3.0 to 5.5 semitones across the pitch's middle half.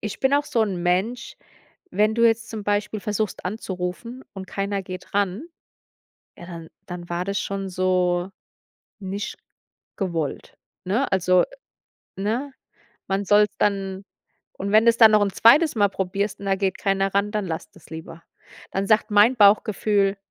No: narrow, 2.5 semitones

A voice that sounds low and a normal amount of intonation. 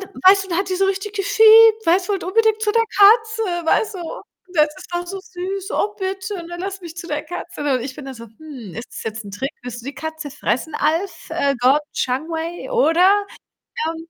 No: very high, 355 Hz; average, 4.9 semitones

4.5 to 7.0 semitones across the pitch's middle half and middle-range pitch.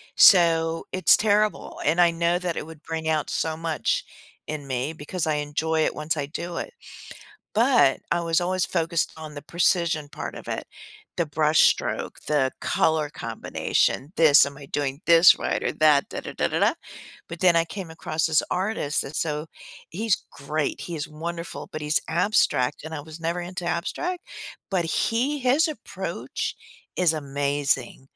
No: narrow, 2.6 semitones; medium, 160 Hz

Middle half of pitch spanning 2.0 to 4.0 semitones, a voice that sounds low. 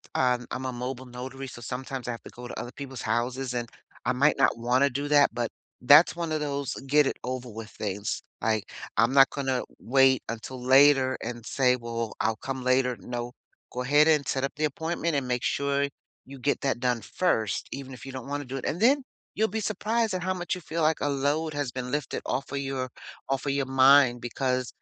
Yes: narrow, 2.6 semitones; low, 130 Hz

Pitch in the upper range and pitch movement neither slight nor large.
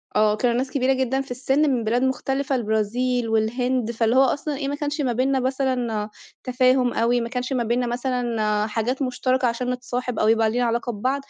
No: very high, 250 Hz; narrow, 2.1 semitones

